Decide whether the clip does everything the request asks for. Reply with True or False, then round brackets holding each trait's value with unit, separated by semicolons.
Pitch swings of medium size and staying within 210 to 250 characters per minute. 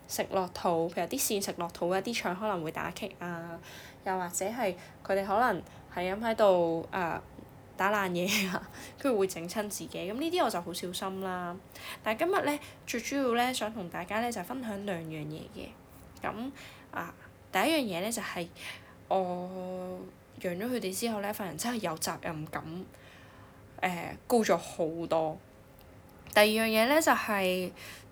True (4.1 semitones; 245 characters per minute)